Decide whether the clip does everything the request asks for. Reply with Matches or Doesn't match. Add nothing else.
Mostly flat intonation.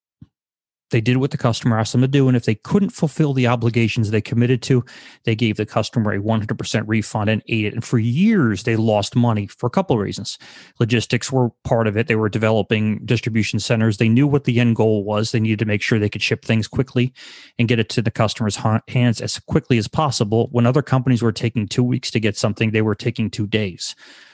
Matches